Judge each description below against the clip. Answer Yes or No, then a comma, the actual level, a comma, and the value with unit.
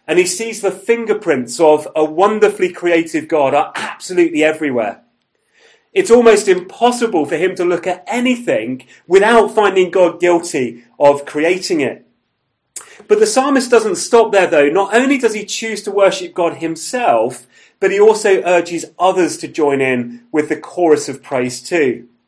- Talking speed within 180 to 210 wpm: No, average, 160 wpm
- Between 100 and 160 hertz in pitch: No, medium, 185 Hz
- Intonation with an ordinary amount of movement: No, wide, 6.8 semitones